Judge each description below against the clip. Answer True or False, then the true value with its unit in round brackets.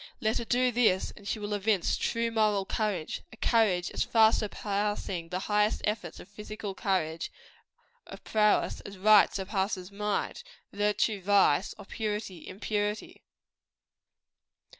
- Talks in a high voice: True (205 Hz)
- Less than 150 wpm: True (135 wpm)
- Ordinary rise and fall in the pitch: False (2.0 semitones)